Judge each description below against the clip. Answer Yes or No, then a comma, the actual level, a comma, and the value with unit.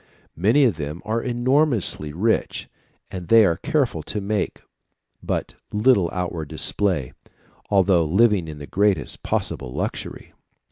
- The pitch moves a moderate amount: No, wide, 5.7 semitones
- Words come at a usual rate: No, slow, 130 wpm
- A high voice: No, low, 100 Hz